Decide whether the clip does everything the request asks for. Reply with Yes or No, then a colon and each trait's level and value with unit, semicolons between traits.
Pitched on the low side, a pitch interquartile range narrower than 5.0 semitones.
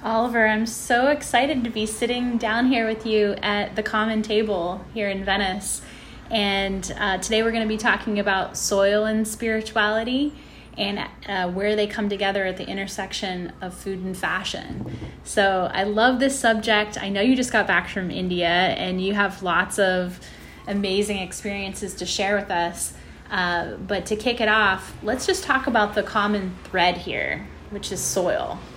No: high, 205 Hz; narrow, 2.5 semitones